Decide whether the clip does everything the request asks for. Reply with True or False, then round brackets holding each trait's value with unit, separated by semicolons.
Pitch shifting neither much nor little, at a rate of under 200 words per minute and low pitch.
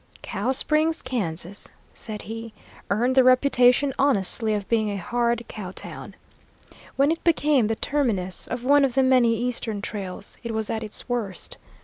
False (3.7 semitones; 160 wpm; 235 Hz)